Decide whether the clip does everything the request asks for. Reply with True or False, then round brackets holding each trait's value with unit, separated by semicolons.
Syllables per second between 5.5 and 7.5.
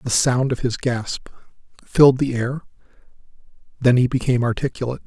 True (5.8 syllables/s)